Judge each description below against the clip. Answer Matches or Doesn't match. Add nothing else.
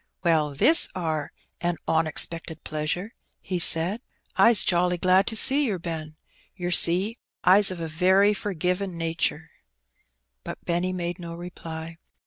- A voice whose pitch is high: Doesn't match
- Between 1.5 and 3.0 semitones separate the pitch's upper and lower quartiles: Matches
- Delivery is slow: Doesn't match